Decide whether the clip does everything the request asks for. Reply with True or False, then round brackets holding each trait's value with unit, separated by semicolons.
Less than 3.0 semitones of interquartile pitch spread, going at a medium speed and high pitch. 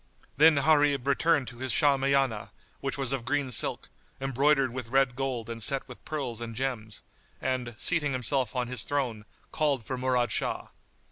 False (2.4 semitones; 165 wpm; 130 Hz)